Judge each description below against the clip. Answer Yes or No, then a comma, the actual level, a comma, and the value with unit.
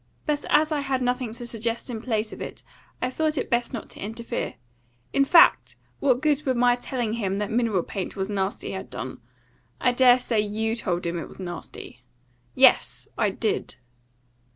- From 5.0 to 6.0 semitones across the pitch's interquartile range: No, average, 3.5 semitones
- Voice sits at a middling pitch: No, high, 235 Hz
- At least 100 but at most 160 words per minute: No, average, 185 wpm